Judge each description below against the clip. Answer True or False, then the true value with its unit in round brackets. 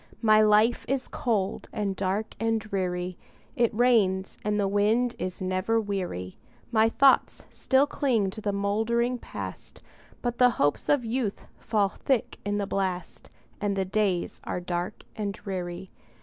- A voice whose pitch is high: True (205 Hz)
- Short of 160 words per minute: True (150 wpm)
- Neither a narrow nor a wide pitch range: True (3.2 semitones)